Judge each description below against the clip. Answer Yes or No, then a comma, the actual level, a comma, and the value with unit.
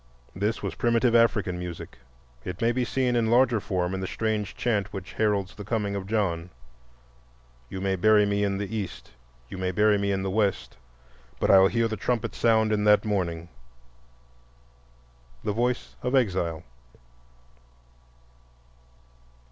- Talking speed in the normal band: Yes, average, 150 wpm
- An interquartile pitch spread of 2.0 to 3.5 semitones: Yes, average, 2.9 semitones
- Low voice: Yes, low, 105 Hz